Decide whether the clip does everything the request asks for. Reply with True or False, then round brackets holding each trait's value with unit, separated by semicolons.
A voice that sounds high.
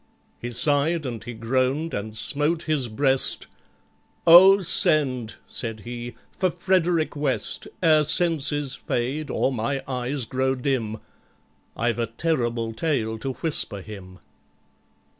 False (130 Hz)